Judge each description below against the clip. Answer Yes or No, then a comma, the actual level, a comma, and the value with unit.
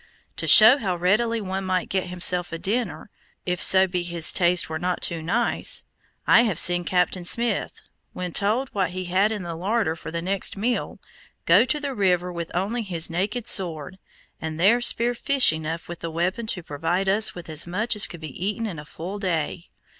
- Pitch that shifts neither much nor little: Yes, average, 3.6 semitones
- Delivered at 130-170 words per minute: No, average, 200 wpm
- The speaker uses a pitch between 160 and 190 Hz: Yes, medium, 185 Hz